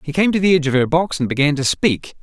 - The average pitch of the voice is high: No, medium, 155 Hz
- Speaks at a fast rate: Yes, fast, 325 wpm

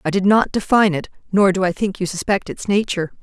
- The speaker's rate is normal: No, fast, 240 wpm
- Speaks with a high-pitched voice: Yes, high, 195 Hz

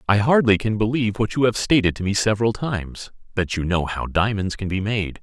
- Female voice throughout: No, male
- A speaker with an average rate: No, fast, 220 wpm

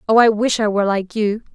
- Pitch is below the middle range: No, high, 215 Hz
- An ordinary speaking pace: No, fast, 235 wpm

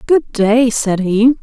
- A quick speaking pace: No, average, 170 wpm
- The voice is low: No, high, 235 Hz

